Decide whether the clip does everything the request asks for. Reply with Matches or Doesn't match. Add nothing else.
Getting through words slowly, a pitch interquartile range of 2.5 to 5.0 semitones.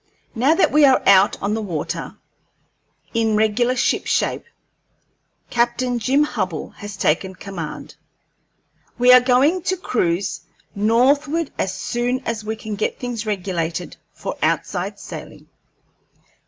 Matches